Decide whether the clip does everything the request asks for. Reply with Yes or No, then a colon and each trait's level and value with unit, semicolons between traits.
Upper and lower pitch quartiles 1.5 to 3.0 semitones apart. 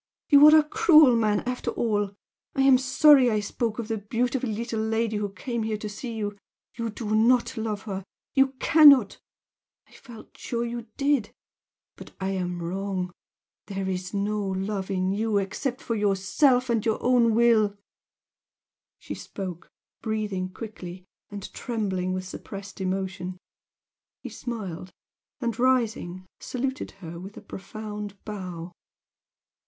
No: average, 3.7 semitones